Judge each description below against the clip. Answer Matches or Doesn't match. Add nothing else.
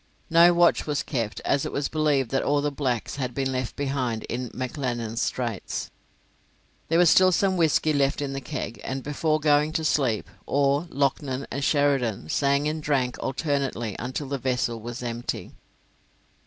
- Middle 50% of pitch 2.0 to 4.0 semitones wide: Matches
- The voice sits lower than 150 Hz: Matches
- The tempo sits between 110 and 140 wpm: Doesn't match